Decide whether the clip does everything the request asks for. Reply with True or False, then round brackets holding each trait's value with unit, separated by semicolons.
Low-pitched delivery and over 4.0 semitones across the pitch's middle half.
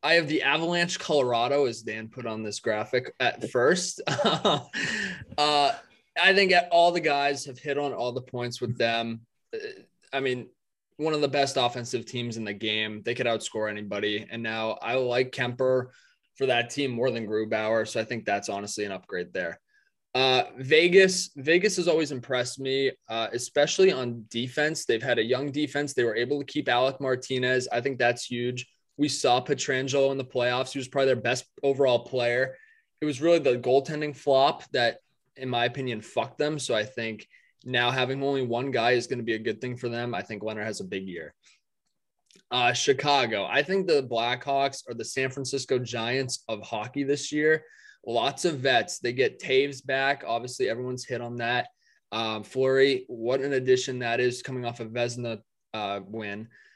False (130 Hz; 3.1 semitones)